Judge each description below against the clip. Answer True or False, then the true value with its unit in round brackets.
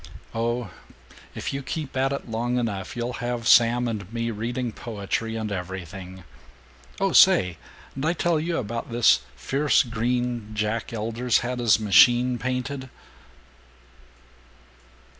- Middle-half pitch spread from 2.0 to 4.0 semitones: True (2.6 semitones)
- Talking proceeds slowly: True (130 wpm)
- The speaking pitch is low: True (120 Hz)